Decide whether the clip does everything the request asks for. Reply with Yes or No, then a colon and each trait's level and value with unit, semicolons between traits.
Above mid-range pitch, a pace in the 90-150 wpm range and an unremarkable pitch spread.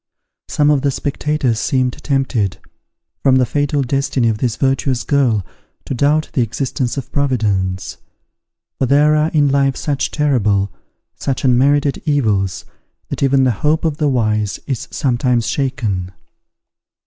No: low, 135 Hz; average, 140 wpm; average, 3.5 semitones